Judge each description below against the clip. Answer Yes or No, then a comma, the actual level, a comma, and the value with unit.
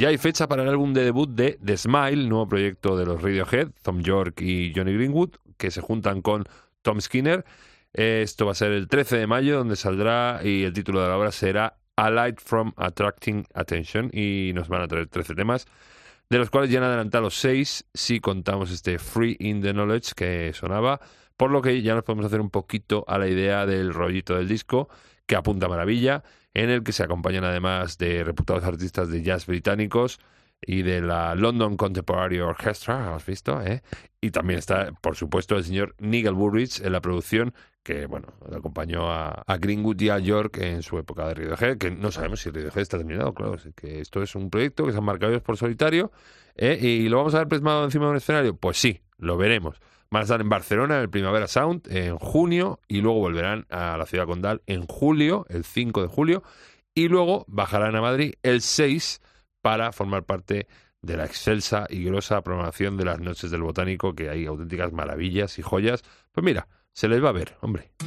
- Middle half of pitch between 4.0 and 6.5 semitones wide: Yes, average, 4.4 semitones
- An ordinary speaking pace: No, fast, 205 wpm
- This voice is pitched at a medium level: No, low, 100 Hz